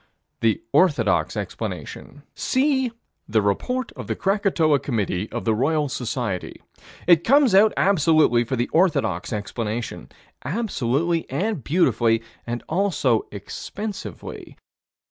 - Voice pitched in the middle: Yes, medium, 145 Hz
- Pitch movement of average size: No, wide, 8.9 semitones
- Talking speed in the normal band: No, slow, 105 wpm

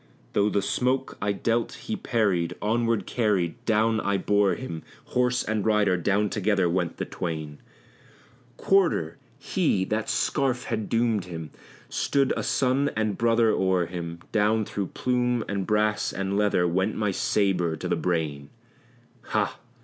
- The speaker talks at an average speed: Yes, average, 150 wpm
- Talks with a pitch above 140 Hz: No, low, 105 Hz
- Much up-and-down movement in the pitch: No, average, 3.9 semitones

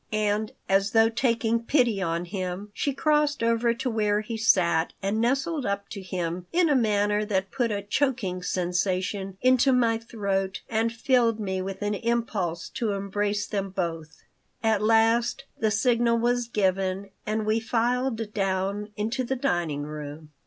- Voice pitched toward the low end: No, high, 210 Hz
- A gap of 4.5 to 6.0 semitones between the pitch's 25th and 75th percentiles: No, average, 3.4 semitones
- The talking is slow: No, average, 160 wpm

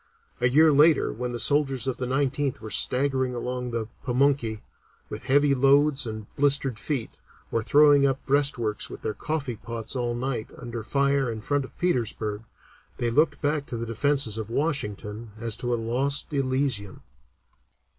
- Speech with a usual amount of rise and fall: Yes, average, 3.5 semitones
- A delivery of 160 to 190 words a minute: Yes, average, 165 wpm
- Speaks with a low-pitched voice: Yes, low, 130 Hz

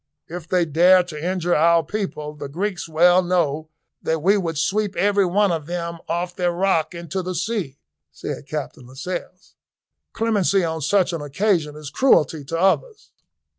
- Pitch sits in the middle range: Yes, medium, 175 Hz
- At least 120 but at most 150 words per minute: No, average, 165 wpm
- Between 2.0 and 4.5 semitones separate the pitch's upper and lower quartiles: Yes, average, 3.3 semitones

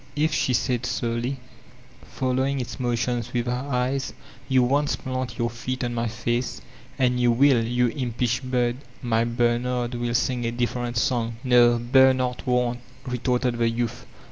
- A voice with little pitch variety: Yes, narrow, 1.3 semitones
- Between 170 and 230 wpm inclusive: No, average, 155 wpm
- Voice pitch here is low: Yes, low, 125 Hz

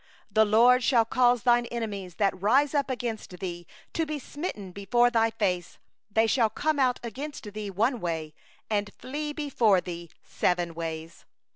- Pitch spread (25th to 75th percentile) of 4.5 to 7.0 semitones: Yes, average, 4.8 semitones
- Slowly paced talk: No, average, 160 wpm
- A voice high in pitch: Yes, high, 225 Hz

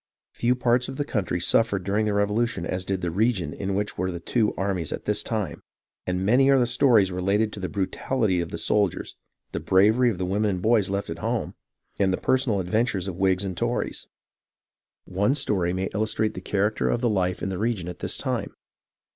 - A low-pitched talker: Yes, low, 100 Hz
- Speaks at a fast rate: Yes, fast, 210 wpm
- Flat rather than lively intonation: No, average, 3.4 semitones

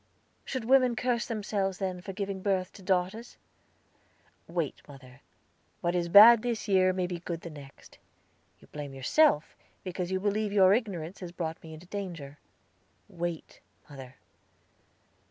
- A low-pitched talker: No, medium, 185 Hz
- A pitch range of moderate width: Yes, average, 3.6 semitones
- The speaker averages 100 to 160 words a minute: Yes, average, 145 wpm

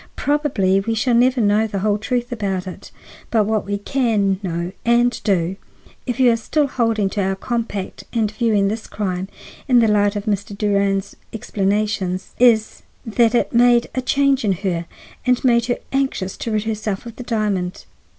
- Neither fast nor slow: Yes, average, 180 wpm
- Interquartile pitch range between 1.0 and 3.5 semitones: Yes, average, 3.2 semitones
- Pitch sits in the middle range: No, high, 215 Hz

